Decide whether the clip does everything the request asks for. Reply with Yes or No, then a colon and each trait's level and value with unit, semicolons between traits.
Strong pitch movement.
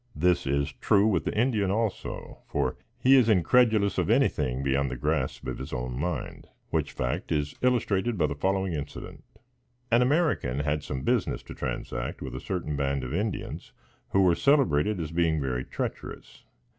Yes: wide, 7.5 semitones